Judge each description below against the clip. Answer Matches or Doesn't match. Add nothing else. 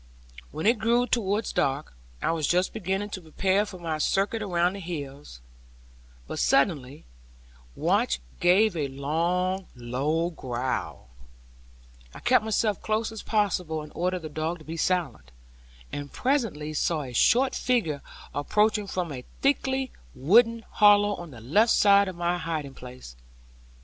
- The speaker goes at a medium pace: Matches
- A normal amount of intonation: Doesn't match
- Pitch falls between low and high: Matches